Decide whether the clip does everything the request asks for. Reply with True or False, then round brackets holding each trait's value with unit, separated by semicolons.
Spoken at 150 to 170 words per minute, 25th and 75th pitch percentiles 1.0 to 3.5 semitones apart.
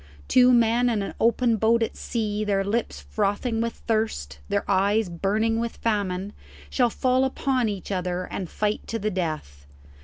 True (165 wpm; 3.0 semitones)